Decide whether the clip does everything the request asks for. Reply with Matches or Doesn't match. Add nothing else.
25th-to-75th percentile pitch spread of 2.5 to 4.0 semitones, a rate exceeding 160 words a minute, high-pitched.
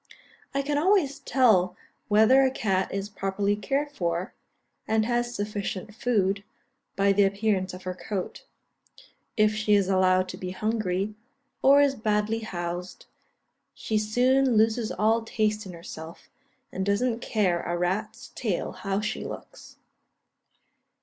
Doesn't match